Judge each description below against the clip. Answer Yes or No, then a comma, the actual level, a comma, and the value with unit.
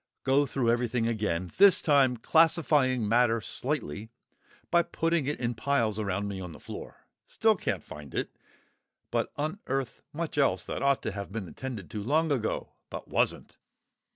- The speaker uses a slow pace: No, average, 160 wpm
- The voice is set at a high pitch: No, low, 125 Hz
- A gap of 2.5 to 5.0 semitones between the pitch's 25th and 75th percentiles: No, wide, 5.5 semitones